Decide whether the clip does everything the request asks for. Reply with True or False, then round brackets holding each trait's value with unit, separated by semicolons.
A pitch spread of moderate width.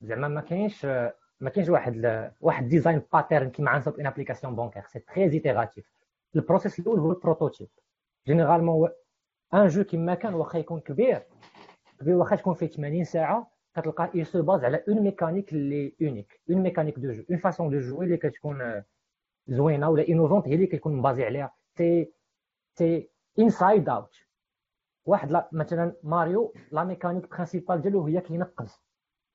True (3.4 semitones)